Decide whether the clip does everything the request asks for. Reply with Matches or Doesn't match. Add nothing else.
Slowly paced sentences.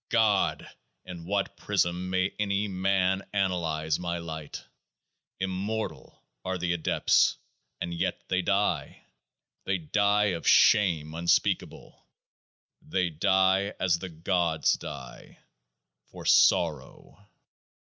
Matches